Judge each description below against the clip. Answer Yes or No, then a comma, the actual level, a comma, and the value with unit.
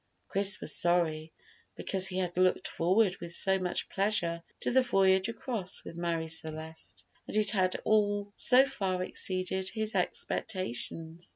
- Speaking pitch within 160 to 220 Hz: Yes, medium, 185 Hz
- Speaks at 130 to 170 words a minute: Yes, average, 150 wpm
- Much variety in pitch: No, average, 3.2 semitones